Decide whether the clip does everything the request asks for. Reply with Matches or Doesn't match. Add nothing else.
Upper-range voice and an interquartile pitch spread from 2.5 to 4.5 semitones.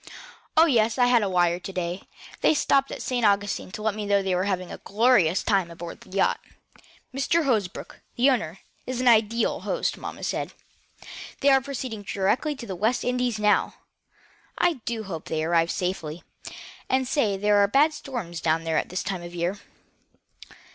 Doesn't match